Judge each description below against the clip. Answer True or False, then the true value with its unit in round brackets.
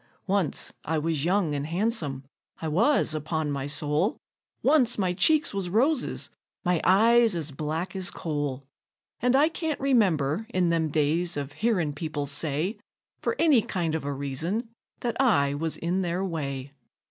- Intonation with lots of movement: True (6.6 semitones)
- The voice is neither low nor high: True (170 Hz)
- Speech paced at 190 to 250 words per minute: False (160 wpm)